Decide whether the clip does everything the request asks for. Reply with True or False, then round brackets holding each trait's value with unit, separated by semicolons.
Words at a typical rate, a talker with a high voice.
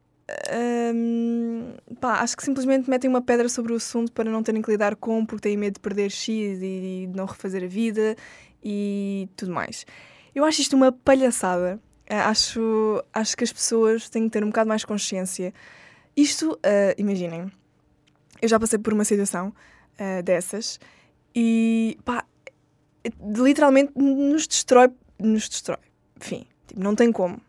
True (160 wpm; 220 Hz)